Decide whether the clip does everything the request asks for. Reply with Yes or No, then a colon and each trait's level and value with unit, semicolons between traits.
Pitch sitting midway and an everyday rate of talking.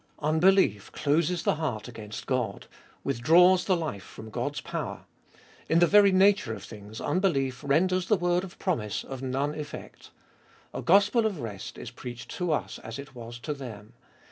Yes: medium, 150 Hz; average, 170 wpm